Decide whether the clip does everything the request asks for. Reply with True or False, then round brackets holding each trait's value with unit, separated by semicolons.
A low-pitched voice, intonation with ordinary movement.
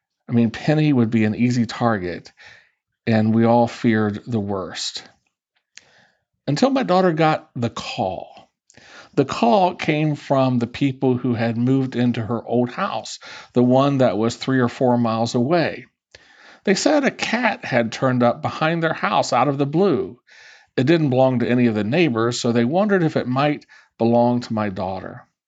True (125 Hz; 3.7 semitones)